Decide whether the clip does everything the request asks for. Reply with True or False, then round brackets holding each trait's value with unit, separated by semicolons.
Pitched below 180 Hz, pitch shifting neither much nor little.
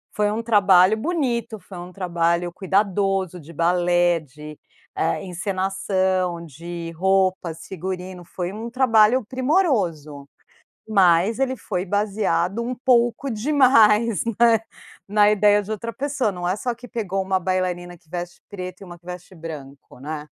False (190 Hz; 3.9 semitones)